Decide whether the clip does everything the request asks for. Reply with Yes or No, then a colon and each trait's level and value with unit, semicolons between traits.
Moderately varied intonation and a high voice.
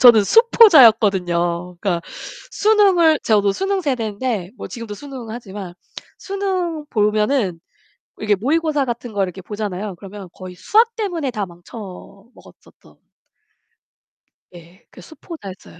No: wide, 8.6 semitones; high, 220 Hz